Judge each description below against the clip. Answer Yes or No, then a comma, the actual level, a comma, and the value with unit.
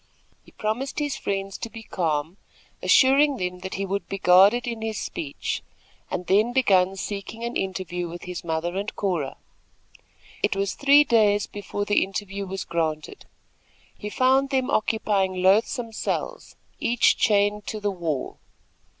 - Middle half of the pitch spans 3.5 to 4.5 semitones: Yes, average, 3.8 semitones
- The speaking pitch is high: Yes, high, 200 Hz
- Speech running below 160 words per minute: Yes, average, 150 wpm